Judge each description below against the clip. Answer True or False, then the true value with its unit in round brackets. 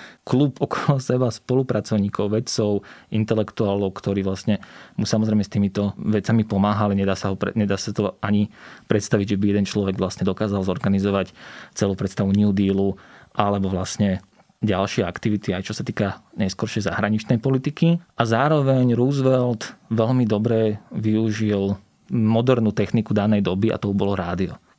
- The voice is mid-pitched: False (105 Hz)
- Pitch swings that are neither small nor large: False (2.3 semitones)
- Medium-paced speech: True (135 wpm)